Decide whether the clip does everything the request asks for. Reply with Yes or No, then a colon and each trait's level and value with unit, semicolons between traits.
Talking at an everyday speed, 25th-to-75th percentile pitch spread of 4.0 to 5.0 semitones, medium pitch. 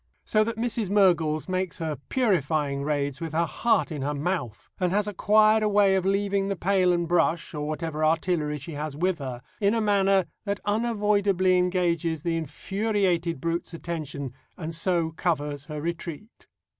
Yes: average, 170 wpm; average, 4.3 semitones; medium, 175 Hz